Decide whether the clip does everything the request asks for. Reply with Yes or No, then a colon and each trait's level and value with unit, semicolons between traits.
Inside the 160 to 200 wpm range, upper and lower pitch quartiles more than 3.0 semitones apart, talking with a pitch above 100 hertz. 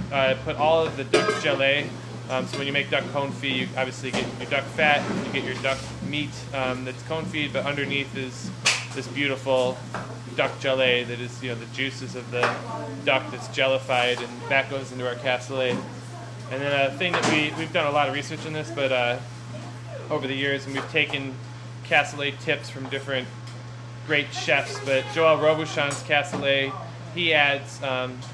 No: average, 185 wpm; narrow, 2.4 semitones; low, 135 Hz